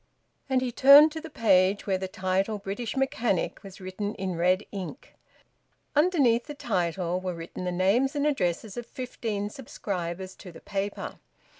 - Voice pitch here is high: Yes, high, 200 Hz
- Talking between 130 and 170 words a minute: Yes, average, 160 wpm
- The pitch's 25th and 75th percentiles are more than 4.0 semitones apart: Yes, average, 5.2 semitones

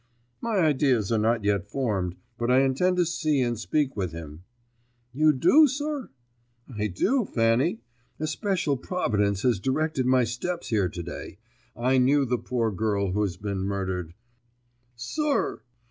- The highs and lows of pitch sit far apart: Yes, wide, 7.1 semitones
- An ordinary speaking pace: Yes, average, 155 wpm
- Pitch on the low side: Yes, low, 120 Hz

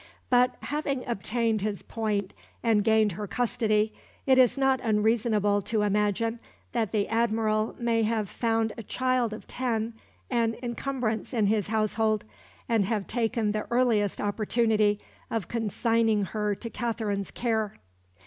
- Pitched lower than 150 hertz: No, high, 220 Hz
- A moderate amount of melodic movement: No, narrow, 1.9 semitones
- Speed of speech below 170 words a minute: Yes, average, 140 wpm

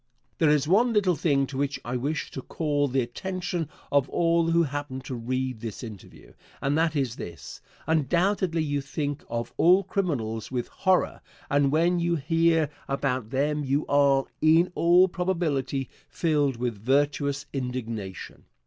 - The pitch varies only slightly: No, average, 4.2 semitones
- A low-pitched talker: No, medium, 145 Hz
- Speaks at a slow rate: No, average, 155 wpm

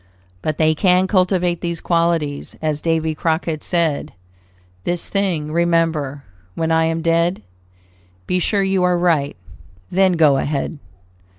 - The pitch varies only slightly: Yes, narrow, 2.3 semitones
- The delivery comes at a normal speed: No, slow, 130 wpm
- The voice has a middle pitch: Yes, medium, 165 Hz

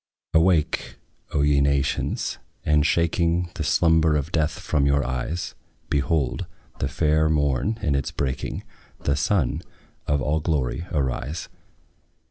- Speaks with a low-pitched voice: Yes, very low, 75 Hz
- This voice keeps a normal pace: No, slow, 125 wpm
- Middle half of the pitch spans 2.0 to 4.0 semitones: Yes, narrow, 2.6 semitones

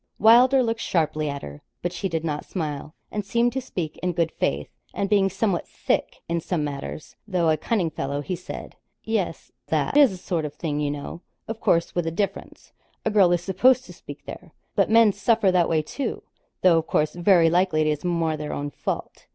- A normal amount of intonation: Yes, average, 4.5 semitones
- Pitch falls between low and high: Yes, medium, 175 Hz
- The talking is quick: Yes, fast, 210 wpm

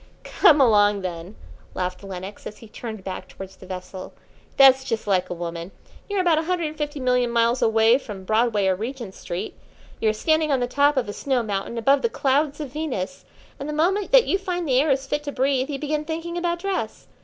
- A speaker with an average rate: No, fast, 220 wpm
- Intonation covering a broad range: Yes, wide, 6.7 semitones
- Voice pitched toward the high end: Yes, very high, 255 Hz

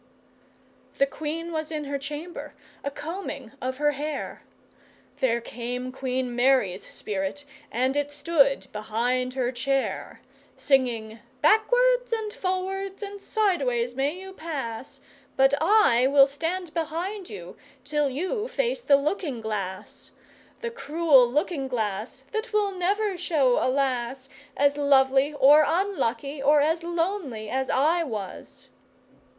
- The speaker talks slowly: Yes, slow, 130 wpm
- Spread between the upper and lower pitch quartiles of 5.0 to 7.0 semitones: Yes, average, 5.3 semitones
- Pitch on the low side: No, very high, 285 Hz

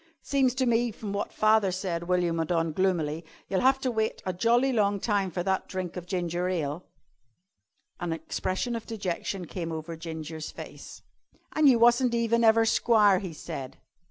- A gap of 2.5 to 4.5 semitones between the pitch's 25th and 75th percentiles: No, average, 5.1 semitones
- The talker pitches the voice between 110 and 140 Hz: No, high, 190 Hz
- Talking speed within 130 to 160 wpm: No, average, 175 wpm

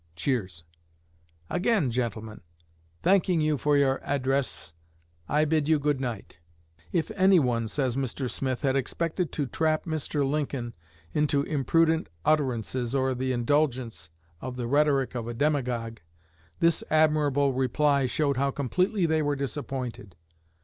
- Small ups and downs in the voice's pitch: No, average, 3.5 semitones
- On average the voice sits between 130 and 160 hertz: Yes, medium, 140 Hz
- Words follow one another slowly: Yes, slow, 130 wpm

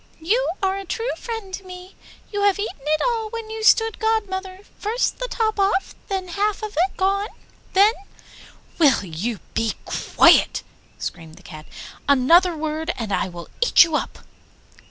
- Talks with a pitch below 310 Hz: No, very high, 380 Hz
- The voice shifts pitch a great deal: Yes, wide, 5.7 semitones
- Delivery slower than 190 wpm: Yes, average, 170 wpm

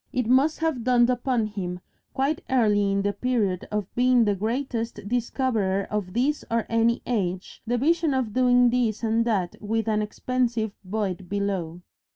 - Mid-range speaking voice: No, high, 230 Hz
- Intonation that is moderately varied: Yes, average, 3.6 semitones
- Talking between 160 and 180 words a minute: Yes, average, 165 wpm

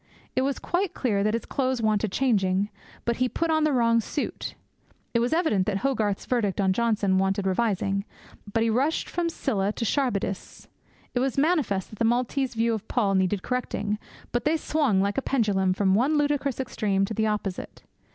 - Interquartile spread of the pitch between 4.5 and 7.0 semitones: Yes, average, 5.0 semitones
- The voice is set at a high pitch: Yes, high, 230 Hz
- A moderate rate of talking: Yes, average, 190 wpm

